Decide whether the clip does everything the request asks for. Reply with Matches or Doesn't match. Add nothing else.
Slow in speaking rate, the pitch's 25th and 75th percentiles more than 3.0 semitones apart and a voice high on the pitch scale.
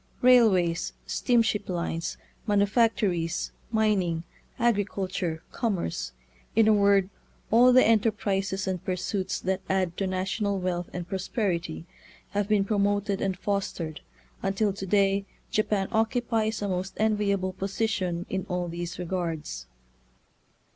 Doesn't match